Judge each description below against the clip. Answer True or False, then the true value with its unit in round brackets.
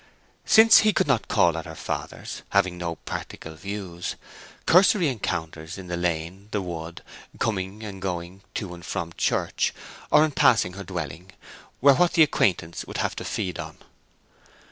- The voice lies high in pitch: False (95 Hz)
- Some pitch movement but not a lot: True (4.0 semitones)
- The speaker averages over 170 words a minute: False (165 wpm)